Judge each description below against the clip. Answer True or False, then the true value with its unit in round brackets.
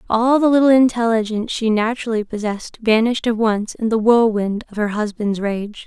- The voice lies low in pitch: False (225 Hz)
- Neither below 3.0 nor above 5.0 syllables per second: False (5.5 syllables/s)